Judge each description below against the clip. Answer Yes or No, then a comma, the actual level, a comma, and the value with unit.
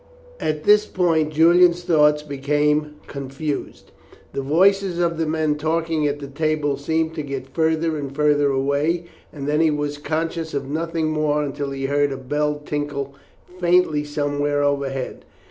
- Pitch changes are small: Yes, narrow, 2.0 semitones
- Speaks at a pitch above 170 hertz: No, medium, 150 Hz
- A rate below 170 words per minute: Yes, average, 155 wpm